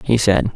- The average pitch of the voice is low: Yes, low, 100 Hz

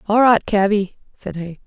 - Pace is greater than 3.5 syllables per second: Yes, 4.6 syllables/s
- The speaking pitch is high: Yes, high, 200 Hz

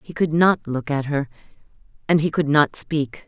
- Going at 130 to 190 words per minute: No, average, 200 wpm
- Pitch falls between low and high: Yes, medium, 150 Hz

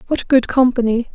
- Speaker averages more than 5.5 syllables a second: No, 5.3 syllables/s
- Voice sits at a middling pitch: No, high, 245 Hz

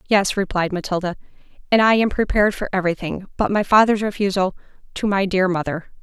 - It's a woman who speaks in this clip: Yes, female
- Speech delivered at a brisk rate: No, average, 180 wpm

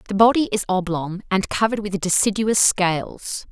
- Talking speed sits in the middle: Yes, average, 155 wpm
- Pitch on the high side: Yes, high, 195 Hz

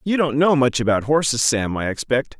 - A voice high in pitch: No, low, 135 Hz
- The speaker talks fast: Yes, fast, 225 wpm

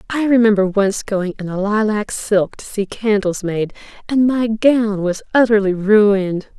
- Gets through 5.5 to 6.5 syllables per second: No, 4.3 syllables/s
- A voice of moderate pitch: No, high, 210 Hz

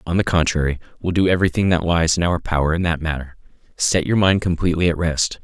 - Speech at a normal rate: No, fast, 220 wpm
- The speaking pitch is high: No, very low, 85 Hz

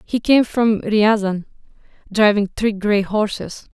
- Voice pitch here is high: Yes, high, 210 Hz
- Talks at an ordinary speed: No, slow, 130 wpm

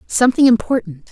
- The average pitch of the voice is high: Yes, high, 225 Hz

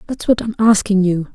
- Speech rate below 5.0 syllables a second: No, 5.4 syllables/s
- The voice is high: Yes, high, 210 Hz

